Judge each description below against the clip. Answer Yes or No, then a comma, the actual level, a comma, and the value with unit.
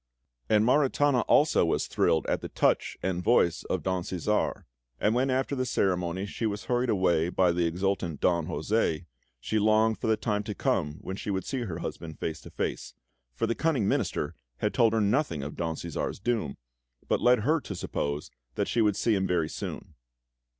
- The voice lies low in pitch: Yes, low, 100 Hz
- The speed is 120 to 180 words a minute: No, average, 195 wpm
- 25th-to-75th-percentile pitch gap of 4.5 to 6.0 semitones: Yes, average, 5.2 semitones